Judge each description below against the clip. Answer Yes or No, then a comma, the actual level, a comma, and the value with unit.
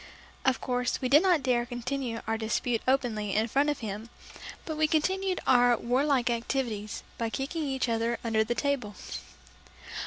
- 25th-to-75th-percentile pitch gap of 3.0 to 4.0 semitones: Yes, average, 3.4 semitones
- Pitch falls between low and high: No, high, 245 Hz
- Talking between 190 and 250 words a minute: No, average, 165 wpm